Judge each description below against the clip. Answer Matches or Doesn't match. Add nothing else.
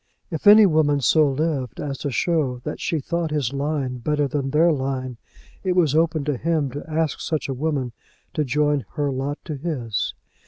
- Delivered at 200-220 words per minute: Doesn't match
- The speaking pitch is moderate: Matches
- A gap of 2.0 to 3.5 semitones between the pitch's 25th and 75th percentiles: Matches